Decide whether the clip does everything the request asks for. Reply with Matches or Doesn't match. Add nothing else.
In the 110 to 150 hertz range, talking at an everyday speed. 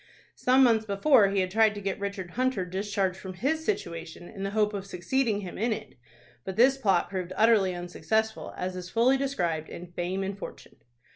Doesn't match